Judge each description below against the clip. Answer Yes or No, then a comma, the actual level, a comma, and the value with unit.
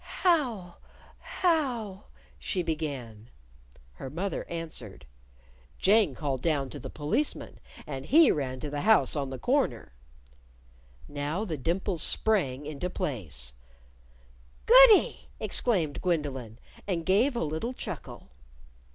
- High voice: No, medium, 160 Hz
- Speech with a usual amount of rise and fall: No, wide, 7.7 semitones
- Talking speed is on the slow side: Yes, slow, 115 wpm